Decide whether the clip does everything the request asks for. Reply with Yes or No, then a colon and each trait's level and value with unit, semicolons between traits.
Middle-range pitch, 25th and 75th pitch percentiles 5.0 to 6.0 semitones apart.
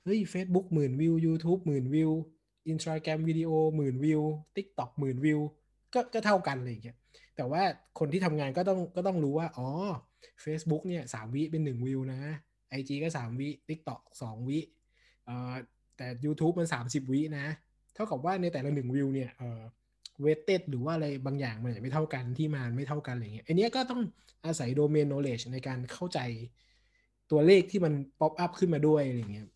No: medium, 150 Hz; average, 4.0 semitones